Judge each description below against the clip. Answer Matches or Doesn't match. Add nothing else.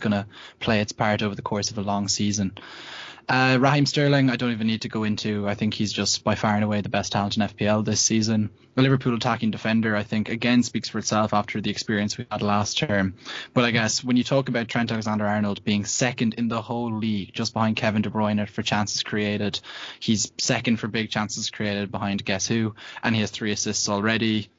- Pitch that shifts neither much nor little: Doesn't match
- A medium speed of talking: Doesn't match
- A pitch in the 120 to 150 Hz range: Doesn't match